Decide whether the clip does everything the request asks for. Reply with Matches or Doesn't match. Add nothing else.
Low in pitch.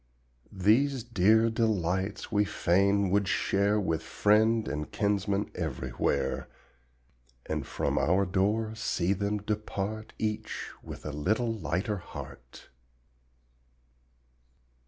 Matches